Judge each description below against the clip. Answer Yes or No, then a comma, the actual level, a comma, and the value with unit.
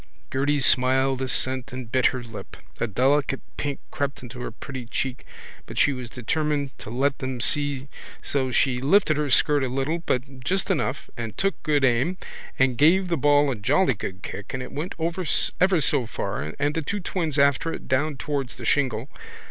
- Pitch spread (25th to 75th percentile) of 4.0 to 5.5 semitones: No, average, 2.7 semitones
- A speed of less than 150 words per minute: No, average, 190 wpm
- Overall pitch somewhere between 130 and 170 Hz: Yes, low, 135 Hz